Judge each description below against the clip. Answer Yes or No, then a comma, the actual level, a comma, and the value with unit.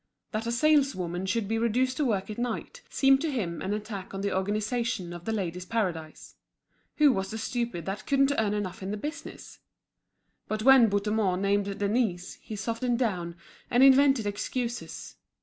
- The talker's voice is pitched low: No, high, 215 Hz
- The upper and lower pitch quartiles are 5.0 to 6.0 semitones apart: No, average, 4.0 semitones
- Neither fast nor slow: Yes, average, 170 wpm